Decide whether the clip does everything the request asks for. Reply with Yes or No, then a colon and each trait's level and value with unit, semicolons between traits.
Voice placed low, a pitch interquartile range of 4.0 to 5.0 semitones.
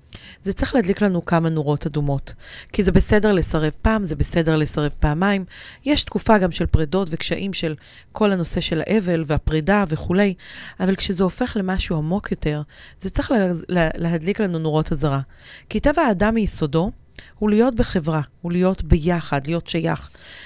No: medium, 175 Hz; average, 4.3 semitones